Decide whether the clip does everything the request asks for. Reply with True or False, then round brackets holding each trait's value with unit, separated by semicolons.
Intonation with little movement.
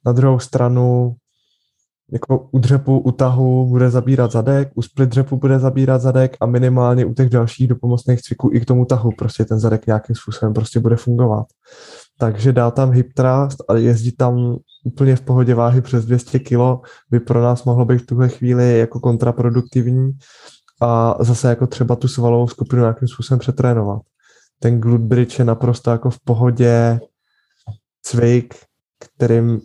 True (1.5 semitones)